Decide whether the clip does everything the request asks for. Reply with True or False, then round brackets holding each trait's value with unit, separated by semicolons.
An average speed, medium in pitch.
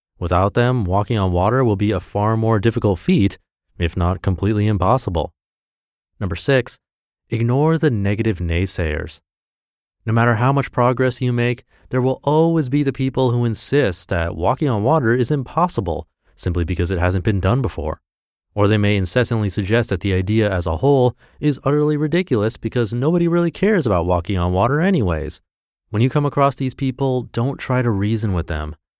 False (175 wpm; 110 Hz)